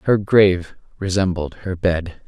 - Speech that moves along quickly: No, slow, 130 wpm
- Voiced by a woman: No, male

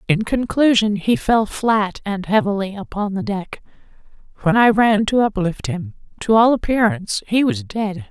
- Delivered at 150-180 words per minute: Yes, average, 165 wpm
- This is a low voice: No, high, 210 Hz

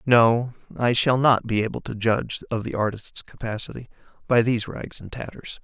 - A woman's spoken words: No, male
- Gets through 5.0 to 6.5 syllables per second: Yes, 5.2 syllables/s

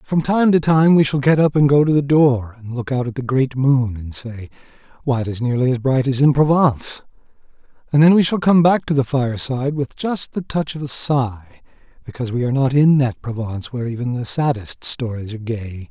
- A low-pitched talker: Yes, low, 130 Hz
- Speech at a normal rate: No, fast, 230 wpm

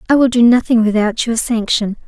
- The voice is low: No, high, 230 Hz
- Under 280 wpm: Yes, average, 200 wpm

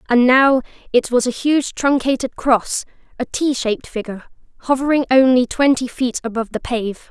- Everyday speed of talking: Yes, average, 160 wpm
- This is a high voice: Yes, very high, 255 Hz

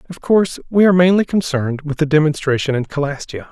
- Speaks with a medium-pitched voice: Yes, medium, 155 Hz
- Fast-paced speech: No, average, 190 wpm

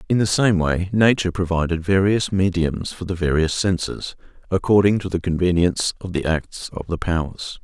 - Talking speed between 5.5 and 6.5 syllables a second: No, 5.2 syllables/s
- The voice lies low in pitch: Yes, very low, 90 Hz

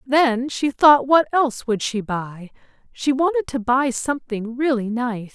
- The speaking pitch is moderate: No, very high, 255 Hz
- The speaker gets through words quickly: No, average, 170 wpm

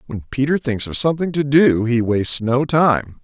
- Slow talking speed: No, fast, 205 wpm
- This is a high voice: No, low, 130 Hz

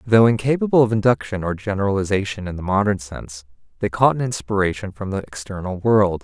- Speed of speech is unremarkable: Yes, average, 175 wpm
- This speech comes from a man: Yes, male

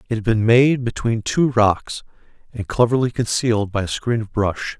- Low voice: Yes, low, 115 Hz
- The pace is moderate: Yes, average, 190 wpm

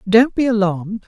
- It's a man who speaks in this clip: No, female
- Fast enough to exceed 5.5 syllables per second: No, 5.3 syllables/s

